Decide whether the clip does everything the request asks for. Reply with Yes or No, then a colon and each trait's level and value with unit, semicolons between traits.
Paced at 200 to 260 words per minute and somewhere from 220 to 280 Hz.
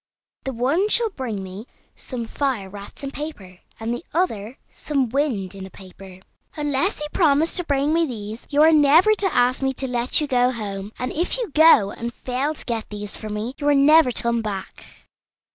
Yes: fast, 205 wpm; very high, 255 Hz